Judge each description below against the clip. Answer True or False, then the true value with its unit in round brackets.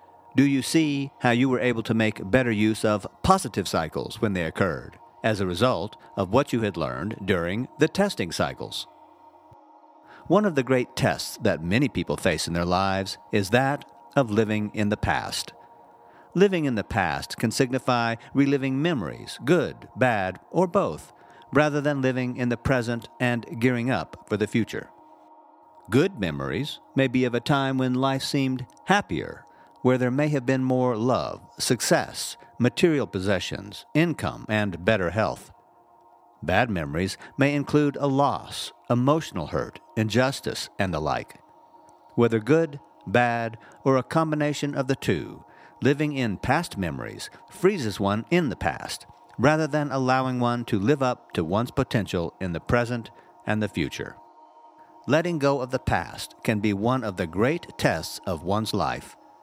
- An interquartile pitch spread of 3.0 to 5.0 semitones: True (4.6 semitones)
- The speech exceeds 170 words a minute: False (160 wpm)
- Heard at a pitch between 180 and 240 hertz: False (125 Hz)